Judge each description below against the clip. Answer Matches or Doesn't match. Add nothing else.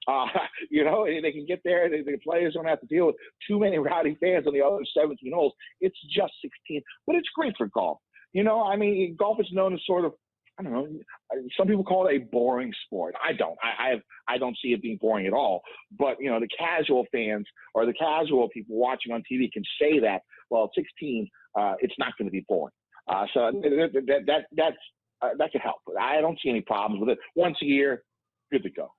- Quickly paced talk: Matches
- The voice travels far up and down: Matches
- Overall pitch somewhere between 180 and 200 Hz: Doesn't match